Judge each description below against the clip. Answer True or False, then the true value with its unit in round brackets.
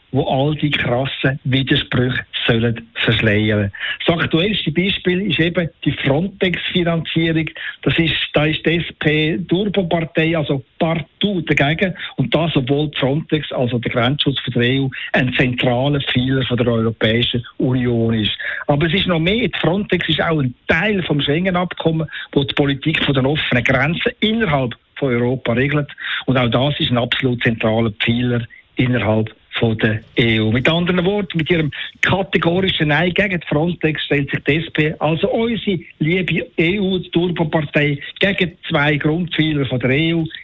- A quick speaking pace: False (145 wpm)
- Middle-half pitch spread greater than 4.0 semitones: True (4.8 semitones)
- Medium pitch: True (150 Hz)